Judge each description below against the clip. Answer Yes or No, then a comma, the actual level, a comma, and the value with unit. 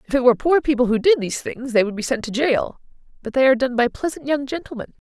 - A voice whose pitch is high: Yes, very high, 250 Hz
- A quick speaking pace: Yes, fast, 270 wpm